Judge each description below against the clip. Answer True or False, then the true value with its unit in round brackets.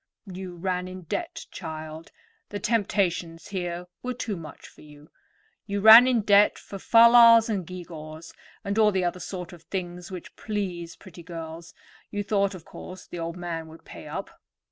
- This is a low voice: False (180 Hz)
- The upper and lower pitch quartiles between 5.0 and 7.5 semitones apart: False (3.4 semitones)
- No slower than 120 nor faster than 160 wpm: False (180 wpm)